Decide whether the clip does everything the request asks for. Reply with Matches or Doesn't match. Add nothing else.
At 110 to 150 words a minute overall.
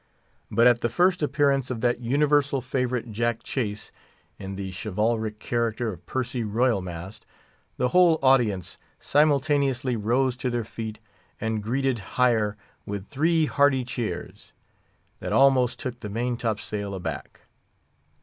Matches